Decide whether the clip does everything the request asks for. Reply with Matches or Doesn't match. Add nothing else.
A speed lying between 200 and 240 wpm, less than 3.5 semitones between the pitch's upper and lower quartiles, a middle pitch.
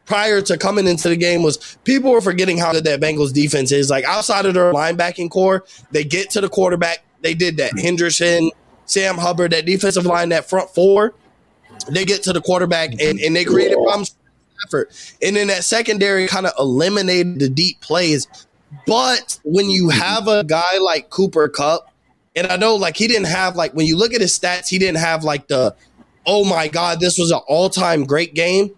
Matches